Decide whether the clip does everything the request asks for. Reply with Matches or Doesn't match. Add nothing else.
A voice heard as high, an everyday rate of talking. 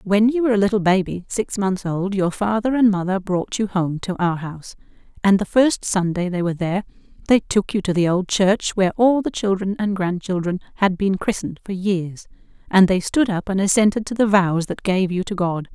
Doesn't match